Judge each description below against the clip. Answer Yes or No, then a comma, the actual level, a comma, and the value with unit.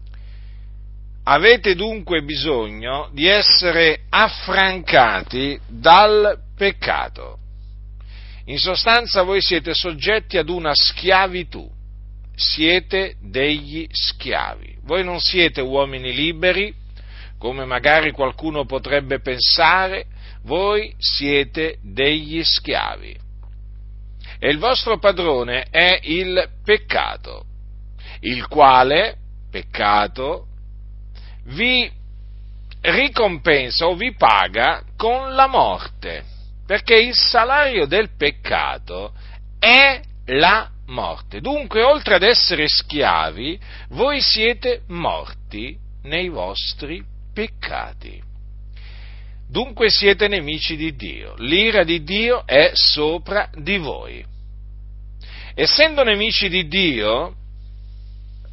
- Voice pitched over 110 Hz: Yes, medium, 140 Hz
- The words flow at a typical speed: No, slow, 90 wpm